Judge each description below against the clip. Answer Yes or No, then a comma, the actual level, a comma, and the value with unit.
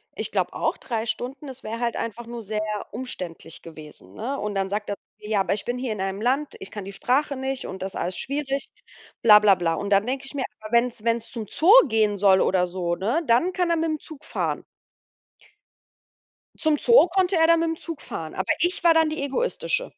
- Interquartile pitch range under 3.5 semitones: No, wide, 6.7 semitones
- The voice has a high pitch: Yes, high, 235 Hz